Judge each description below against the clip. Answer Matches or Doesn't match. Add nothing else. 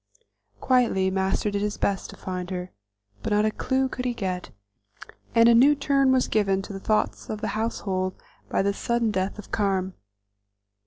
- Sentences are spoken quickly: Doesn't match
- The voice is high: Matches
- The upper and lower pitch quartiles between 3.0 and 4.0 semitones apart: Matches